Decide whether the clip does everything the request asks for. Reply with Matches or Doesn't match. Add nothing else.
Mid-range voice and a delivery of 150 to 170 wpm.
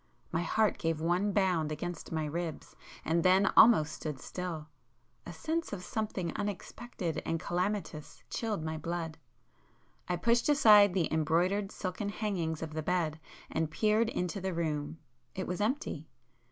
Doesn't match